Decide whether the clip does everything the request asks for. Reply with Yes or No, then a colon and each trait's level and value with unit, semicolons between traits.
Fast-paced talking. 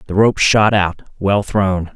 No: average, 185 wpm